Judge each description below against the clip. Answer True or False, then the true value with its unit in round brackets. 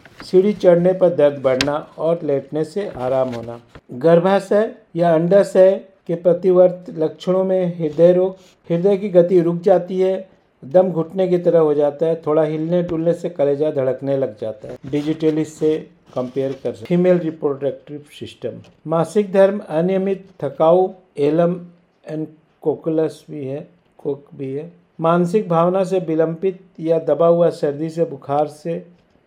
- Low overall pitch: False (170 Hz)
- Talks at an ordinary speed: True (145 wpm)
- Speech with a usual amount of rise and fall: True (3.4 semitones)